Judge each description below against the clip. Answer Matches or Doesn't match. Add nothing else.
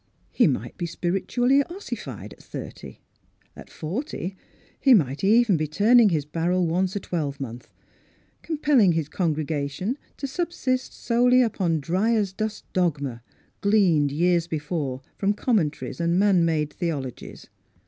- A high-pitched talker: Doesn't match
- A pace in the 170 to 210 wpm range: Doesn't match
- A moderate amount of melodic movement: Doesn't match